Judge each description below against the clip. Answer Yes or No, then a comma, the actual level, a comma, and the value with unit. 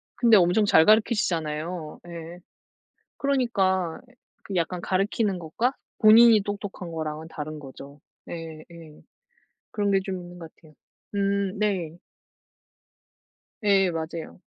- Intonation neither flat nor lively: Yes, average, 4.0 semitones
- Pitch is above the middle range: No, medium, 180 Hz